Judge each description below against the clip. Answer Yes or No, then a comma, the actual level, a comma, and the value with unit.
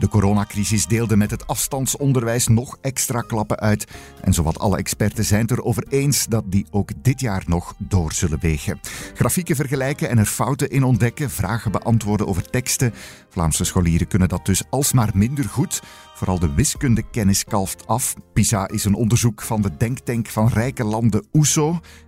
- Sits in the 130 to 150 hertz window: No, low, 110 Hz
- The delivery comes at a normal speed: Yes, average, 170 wpm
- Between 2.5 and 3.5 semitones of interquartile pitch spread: No, average, 4.1 semitones